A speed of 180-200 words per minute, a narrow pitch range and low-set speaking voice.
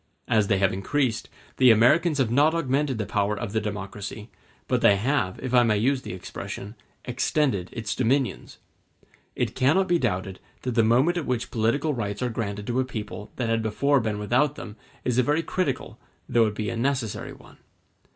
No: average, 190 wpm; average, 4.3 semitones; low, 120 Hz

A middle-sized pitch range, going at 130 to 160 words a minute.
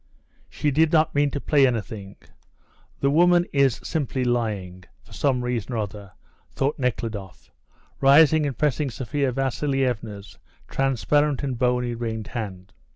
Yes: average, 4.3 semitones; slow, 135 wpm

